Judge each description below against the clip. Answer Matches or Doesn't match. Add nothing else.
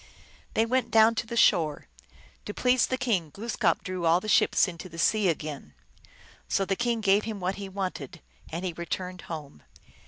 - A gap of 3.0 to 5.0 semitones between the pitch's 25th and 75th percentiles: Matches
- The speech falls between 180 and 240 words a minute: Matches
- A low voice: Doesn't match